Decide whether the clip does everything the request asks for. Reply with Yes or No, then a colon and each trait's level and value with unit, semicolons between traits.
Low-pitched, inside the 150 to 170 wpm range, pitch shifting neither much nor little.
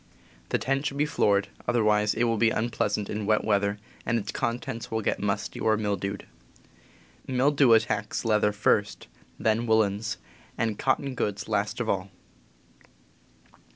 No: low, 110 Hz; average, 155 wpm; narrow, 2.3 semitones